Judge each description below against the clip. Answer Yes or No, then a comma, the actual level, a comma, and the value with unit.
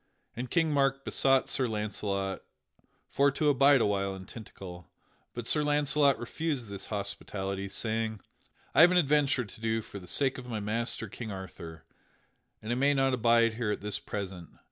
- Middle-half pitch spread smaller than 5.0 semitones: No, wide, 5.4 semitones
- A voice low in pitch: Yes, low, 115 Hz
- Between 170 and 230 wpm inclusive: Yes, average, 175 wpm